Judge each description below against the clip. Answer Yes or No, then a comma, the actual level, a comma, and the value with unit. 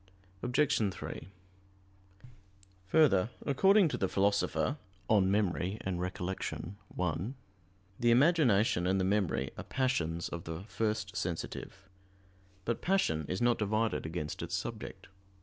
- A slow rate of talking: Yes, slow, 120 wpm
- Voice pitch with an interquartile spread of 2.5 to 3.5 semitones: No, average, 5.0 semitones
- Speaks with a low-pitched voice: Yes, low, 100 Hz